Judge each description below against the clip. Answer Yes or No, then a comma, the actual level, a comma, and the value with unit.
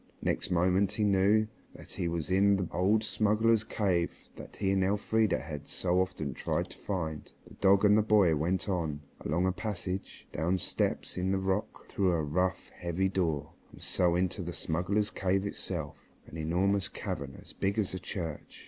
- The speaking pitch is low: Yes, very low, 95 Hz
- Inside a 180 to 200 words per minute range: Yes, average, 185 wpm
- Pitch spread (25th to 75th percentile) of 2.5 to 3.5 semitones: Yes, average, 2.8 semitones